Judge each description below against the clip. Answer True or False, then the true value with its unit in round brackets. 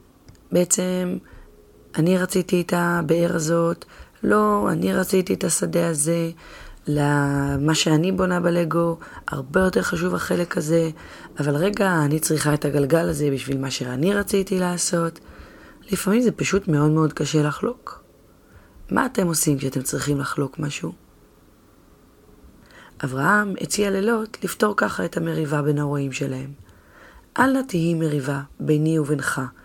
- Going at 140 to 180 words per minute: False (130 wpm)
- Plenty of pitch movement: False (3.9 semitones)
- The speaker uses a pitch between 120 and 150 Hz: False (165 Hz)